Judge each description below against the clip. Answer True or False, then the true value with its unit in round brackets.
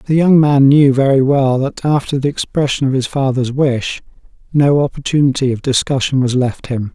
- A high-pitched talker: False (135 Hz)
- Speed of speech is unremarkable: True (180 wpm)